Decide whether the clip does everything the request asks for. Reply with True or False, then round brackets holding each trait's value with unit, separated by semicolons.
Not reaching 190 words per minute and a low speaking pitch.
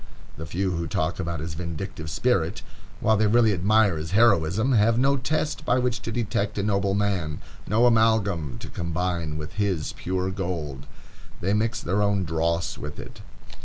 True (170 wpm; 95 Hz)